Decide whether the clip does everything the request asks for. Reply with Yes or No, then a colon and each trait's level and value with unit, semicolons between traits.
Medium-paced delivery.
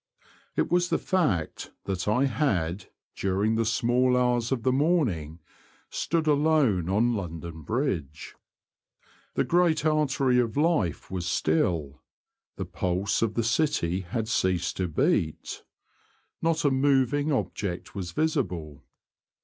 No: slow, 125 wpm